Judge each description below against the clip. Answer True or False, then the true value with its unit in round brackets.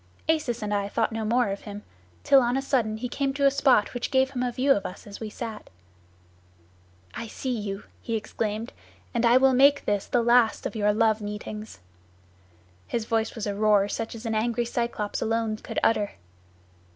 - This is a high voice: True (225 Hz)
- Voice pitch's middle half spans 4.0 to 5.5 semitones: False (2.8 semitones)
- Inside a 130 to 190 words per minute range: False (200 wpm)